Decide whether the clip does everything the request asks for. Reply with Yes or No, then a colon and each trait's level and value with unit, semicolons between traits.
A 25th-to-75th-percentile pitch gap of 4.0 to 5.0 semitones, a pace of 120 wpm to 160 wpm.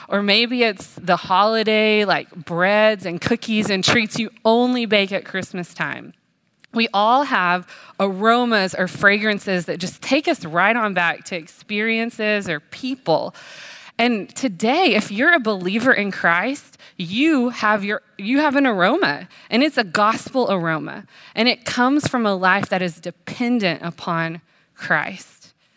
Yes: average, 4.5 semitones; average, 150 wpm